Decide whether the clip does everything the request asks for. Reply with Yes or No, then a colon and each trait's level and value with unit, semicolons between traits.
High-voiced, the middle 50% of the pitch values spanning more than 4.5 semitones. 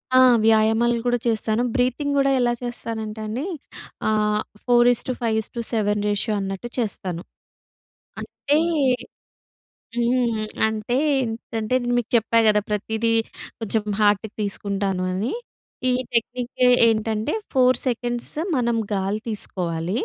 No: high, 225 Hz; narrow, 2.4 semitones